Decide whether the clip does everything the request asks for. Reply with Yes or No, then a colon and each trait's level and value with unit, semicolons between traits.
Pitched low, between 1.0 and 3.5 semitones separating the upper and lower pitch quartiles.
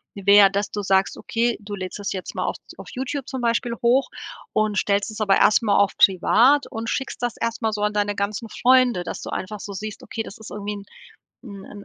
No: high, 210 Hz; narrow, 2.6 semitones